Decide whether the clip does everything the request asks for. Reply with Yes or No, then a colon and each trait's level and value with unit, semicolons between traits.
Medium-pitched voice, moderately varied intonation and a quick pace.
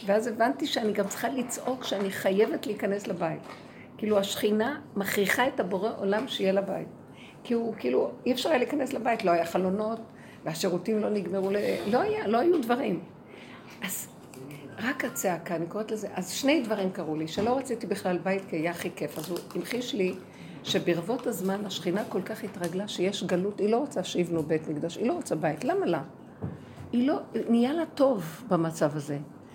No: high, 200 Hz; average, 4.6 semitones; fast, 175 wpm